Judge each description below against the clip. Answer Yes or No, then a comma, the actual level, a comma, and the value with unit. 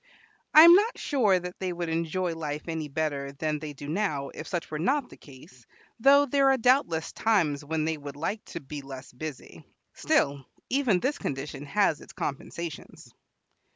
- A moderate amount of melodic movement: No, wide, 6.5 semitones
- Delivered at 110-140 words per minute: No, average, 180 wpm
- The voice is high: No, medium, 160 Hz